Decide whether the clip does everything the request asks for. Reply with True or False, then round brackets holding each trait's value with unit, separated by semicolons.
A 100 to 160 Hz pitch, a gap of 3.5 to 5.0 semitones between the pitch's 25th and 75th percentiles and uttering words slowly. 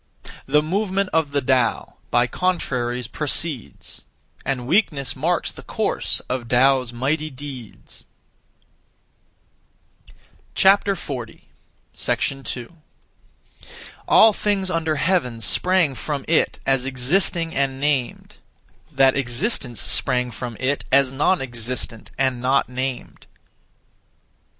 True (135 Hz; 4.4 semitones; 100 wpm)